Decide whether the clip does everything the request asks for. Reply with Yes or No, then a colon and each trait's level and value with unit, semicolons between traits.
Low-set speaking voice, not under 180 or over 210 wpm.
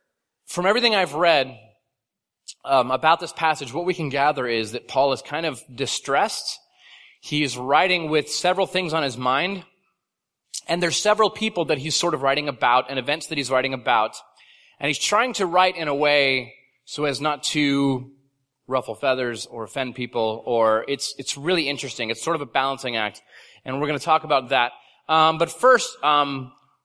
No: medium, 145 Hz; average, 200 wpm